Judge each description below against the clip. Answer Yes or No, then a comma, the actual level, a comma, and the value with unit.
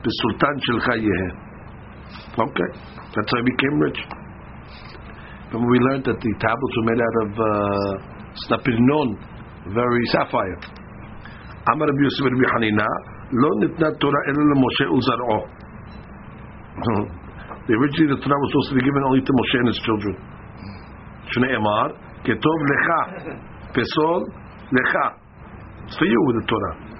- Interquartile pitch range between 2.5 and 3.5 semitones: No, average, 4.0 semitones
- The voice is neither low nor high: No, low, 115 Hz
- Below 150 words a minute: Yes, average, 140 wpm